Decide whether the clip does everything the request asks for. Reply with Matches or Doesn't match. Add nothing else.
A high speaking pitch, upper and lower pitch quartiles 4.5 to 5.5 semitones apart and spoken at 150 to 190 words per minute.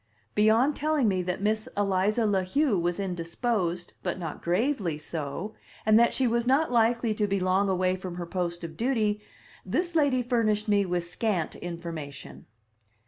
Matches